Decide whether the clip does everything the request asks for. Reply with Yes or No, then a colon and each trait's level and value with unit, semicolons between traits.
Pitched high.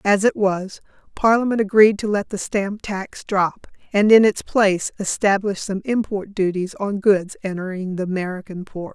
Yes: high, 200 Hz